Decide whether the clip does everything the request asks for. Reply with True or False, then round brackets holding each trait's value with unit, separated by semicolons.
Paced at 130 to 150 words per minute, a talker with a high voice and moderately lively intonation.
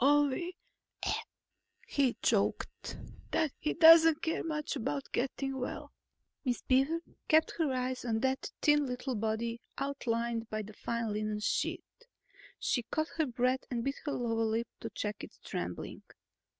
True (145 wpm; 255 Hz; 4.1 semitones)